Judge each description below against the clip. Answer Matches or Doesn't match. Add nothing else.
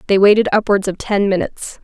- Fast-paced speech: Doesn't match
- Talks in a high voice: Matches